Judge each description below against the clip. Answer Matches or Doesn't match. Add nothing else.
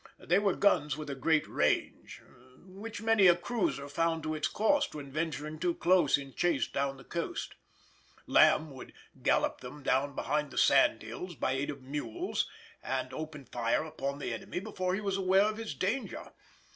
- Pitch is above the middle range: Doesn't match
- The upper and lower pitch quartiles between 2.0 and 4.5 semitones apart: Doesn't match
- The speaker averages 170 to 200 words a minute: Matches